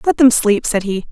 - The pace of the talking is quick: Yes, fast, 270 wpm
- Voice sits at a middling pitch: No, high, 225 Hz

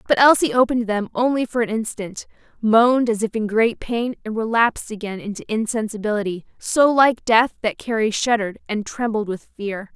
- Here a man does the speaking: No, female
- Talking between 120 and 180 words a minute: Yes, average, 175 wpm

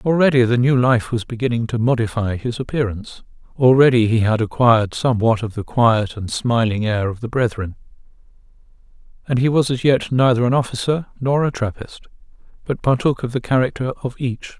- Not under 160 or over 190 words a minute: Yes, average, 175 wpm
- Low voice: Yes, low, 120 Hz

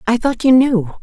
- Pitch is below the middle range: No, high, 230 Hz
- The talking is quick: Yes, fast, 235 wpm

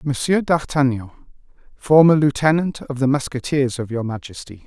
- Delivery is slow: Yes, slow, 130 wpm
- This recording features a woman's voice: No, male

